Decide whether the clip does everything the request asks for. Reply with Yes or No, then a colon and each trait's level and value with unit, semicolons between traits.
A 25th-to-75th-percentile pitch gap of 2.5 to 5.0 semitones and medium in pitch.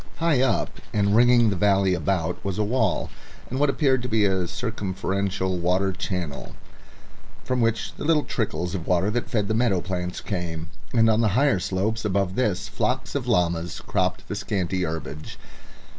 No: average, 4.0 semitones; low, 100 Hz